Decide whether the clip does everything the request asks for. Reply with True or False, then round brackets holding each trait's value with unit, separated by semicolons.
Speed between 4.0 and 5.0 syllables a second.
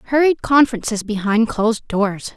False (5.3 syllables/s)